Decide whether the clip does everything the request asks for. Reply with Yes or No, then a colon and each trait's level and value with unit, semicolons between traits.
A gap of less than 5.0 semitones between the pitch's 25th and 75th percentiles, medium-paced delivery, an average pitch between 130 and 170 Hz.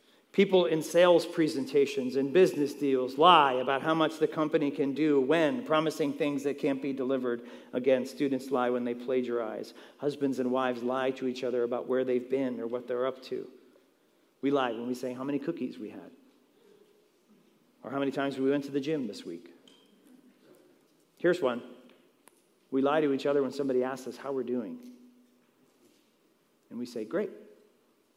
Yes: average, 3.6 semitones; average, 175 wpm; medium, 140 Hz